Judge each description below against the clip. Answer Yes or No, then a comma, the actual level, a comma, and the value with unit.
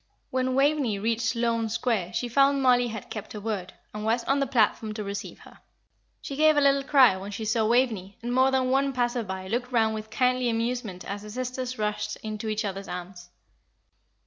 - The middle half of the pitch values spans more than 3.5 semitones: No, average, 3.2 semitones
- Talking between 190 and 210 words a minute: Yes, average, 200 wpm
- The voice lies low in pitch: No, high, 230 Hz